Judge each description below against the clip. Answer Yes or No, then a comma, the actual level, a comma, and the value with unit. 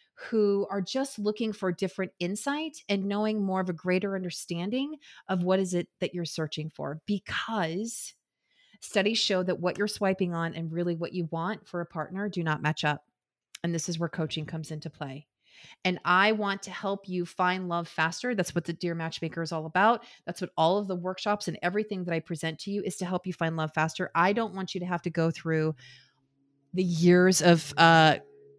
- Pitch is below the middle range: No, medium, 180 Hz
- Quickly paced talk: Yes, fast, 210 wpm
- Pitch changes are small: No, average, 3.3 semitones